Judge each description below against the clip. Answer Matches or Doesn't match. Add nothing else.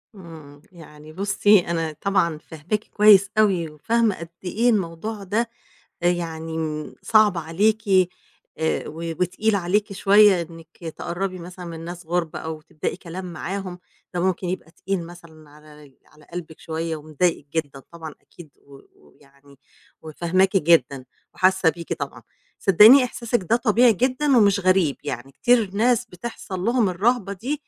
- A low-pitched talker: Doesn't match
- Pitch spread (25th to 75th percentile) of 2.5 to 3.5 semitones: Doesn't match